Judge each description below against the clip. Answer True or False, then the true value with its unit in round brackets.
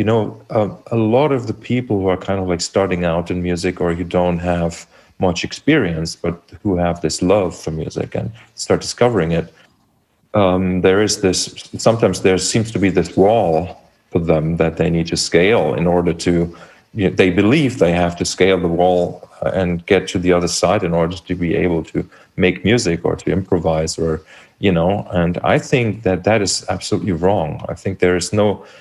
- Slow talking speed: False (205 wpm)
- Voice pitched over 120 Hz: False (90 Hz)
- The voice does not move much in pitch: True (2.2 semitones)